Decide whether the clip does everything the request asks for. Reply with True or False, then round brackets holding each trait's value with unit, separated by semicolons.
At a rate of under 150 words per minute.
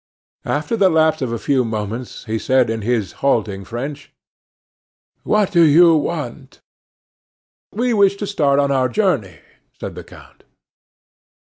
True (140 wpm)